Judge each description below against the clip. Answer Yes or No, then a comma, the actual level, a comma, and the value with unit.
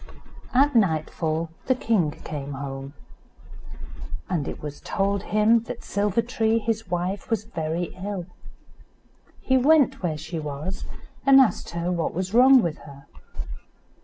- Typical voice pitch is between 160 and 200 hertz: Yes, medium, 185 Hz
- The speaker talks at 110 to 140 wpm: Yes, slow, 135 wpm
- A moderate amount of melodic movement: No, wide, 6.2 semitones